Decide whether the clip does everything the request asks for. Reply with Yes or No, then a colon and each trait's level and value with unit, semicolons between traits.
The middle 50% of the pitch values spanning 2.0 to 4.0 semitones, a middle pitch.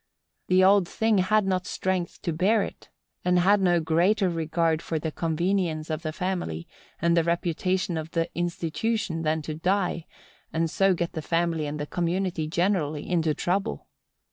Yes: average, 2.8 semitones; medium, 170 Hz